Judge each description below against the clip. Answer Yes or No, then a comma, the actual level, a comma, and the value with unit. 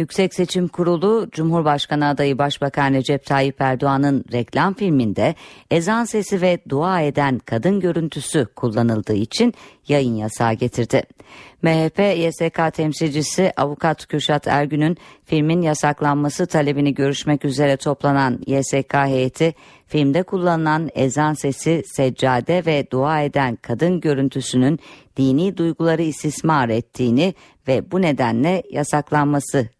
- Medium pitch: Yes, medium, 145 Hz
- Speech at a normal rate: Yes, average, 110 wpm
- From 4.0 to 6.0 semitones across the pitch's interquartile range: No, average, 3.5 semitones